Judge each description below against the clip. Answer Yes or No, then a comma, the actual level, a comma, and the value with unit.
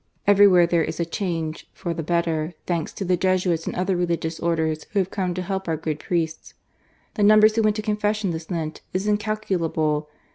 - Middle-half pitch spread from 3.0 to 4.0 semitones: Yes, average, 3.5 semitones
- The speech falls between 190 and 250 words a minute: Yes, average, 195 wpm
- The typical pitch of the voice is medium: Yes, medium, 175 Hz